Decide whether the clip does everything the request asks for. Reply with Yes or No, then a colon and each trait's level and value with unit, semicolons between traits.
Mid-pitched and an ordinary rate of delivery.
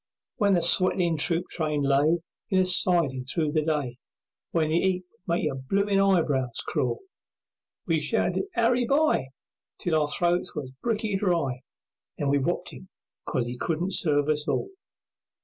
Yes: medium, 165 Hz; average, 160 wpm